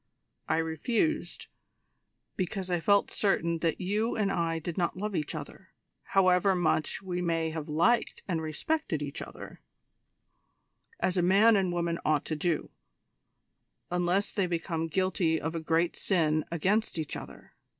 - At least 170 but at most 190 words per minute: No, average, 150 wpm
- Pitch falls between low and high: Yes, medium, 175 Hz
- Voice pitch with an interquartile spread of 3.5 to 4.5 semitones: No, average, 3.0 semitones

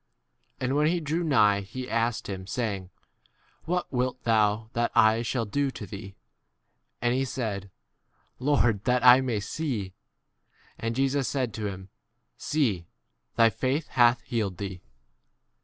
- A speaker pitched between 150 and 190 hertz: No, low, 120 Hz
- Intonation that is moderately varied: Yes, average, 4.2 semitones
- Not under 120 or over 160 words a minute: Yes, average, 155 wpm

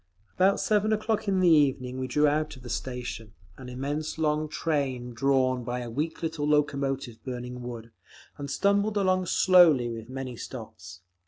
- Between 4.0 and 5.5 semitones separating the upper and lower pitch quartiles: Yes, average, 4.4 semitones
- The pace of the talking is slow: No, average, 165 wpm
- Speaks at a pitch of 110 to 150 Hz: Yes, medium, 140 Hz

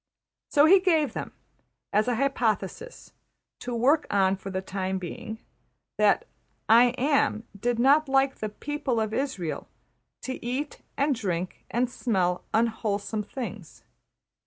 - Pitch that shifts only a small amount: No, average, 5.2 semitones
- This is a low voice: No, high, 235 Hz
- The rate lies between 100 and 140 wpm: Yes, slow, 135 wpm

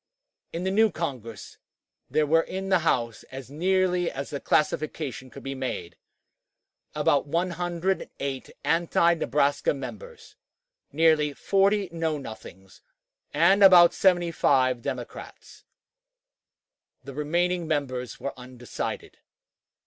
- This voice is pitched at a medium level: Yes, medium, 160 Hz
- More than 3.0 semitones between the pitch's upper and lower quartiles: Yes, average, 4.7 semitones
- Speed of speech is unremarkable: No, slow, 105 wpm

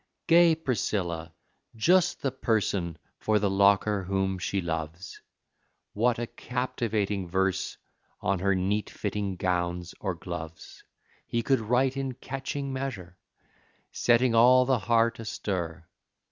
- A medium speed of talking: No, slow, 120 wpm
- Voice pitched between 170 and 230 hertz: No, low, 105 Hz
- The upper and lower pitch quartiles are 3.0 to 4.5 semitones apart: No, average, 5.1 semitones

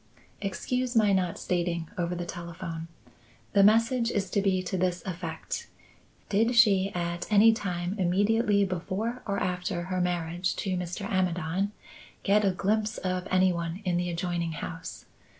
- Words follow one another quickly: No, average, 150 wpm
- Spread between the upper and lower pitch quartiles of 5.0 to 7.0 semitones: No, narrow, 2.6 semitones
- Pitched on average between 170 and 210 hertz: Yes, medium, 185 Hz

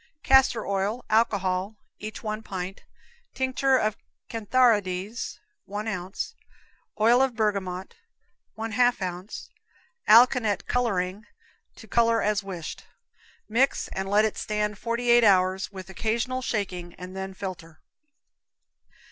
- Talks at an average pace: No, slow, 105 wpm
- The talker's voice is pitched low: No, high, 210 Hz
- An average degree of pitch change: Yes, average, 3.4 semitones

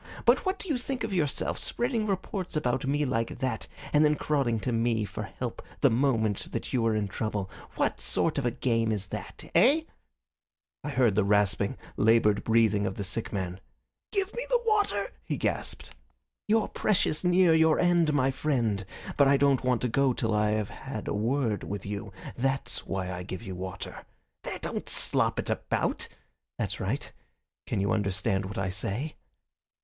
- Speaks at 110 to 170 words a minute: No, average, 185 wpm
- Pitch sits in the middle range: No, low, 120 Hz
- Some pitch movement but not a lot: No, wide, 6.8 semitones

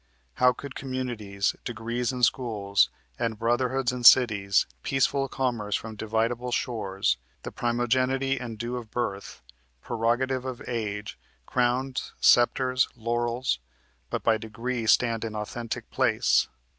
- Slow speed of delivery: Yes, slow, 120 wpm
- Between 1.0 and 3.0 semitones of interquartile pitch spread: Yes, narrow, 2.4 semitones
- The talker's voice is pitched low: Yes, low, 120 Hz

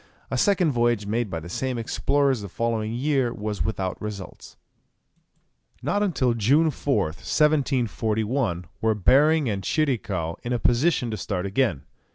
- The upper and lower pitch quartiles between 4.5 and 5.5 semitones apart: Yes, average, 5.1 semitones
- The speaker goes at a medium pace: Yes, average, 145 wpm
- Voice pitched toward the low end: Yes, low, 115 Hz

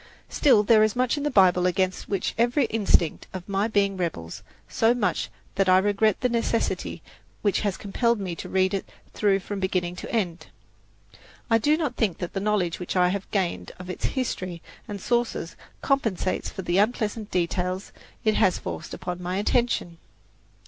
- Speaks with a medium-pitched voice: No, high, 195 Hz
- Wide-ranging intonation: No, average, 3.6 semitones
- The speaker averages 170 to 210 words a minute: Yes, average, 180 wpm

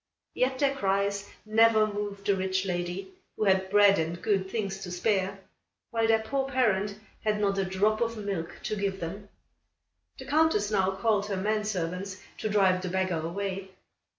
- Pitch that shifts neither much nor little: No, narrow, 2.2 semitones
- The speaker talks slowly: No, average, 175 wpm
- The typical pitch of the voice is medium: No, high, 200 Hz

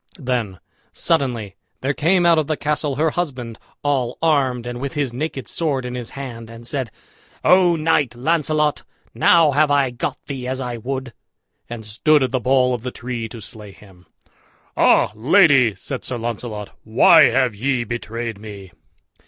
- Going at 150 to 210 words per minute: Yes, average, 170 wpm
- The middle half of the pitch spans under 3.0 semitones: No, average, 3.8 semitones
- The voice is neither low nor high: No, low, 125 Hz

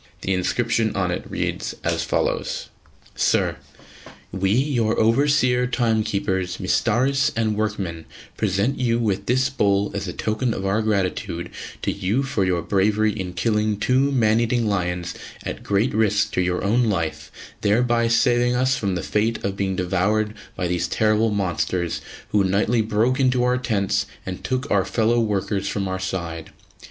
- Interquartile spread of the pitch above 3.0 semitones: Yes, average, 3.7 semitones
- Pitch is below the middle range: Yes, low, 105 Hz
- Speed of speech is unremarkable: Yes, average, 160 wpm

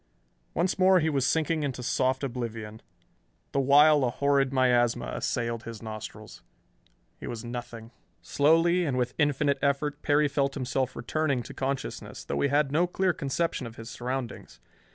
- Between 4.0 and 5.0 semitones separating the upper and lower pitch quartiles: No, average, 3.5 semitones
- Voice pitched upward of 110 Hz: Yes, low, 135 Hz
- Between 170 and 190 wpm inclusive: No, average, 155 wpm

